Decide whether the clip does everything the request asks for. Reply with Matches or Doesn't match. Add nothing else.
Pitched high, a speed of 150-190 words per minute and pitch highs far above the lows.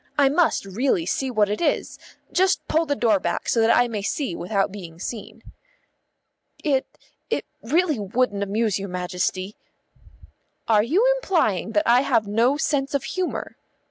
Matches